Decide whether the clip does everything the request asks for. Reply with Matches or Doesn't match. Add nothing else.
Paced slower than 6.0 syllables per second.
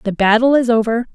Doesn't match